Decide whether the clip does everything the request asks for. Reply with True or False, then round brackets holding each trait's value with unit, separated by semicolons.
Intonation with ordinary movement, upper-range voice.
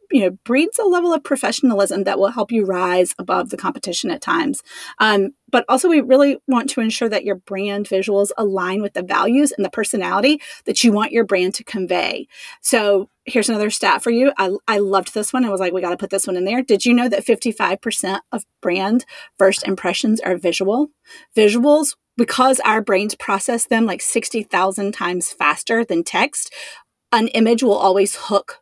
True (3.9 semitones; 215 Hz)